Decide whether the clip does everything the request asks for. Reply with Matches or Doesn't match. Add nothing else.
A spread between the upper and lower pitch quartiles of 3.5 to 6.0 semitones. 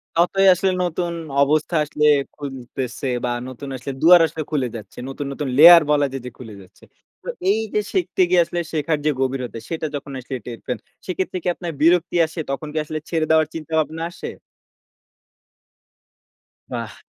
Matches